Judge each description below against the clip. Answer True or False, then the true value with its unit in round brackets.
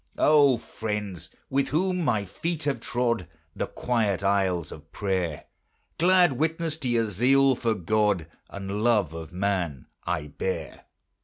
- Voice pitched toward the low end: True (110 Hz)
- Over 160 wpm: False (140 wpm)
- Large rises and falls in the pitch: True (6.5 semitones)